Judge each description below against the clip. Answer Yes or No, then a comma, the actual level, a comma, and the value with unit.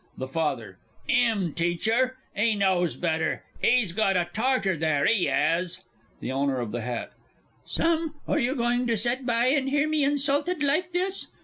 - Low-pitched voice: No, high, 225 Hz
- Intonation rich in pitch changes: Yes, wide, 8.4 semitones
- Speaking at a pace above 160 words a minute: Yes, average, 175 wpm